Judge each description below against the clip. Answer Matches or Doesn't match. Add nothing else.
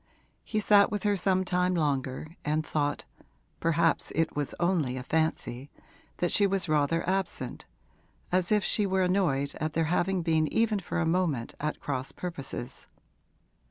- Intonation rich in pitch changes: Doesn't match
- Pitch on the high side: Doesn't match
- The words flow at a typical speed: Matches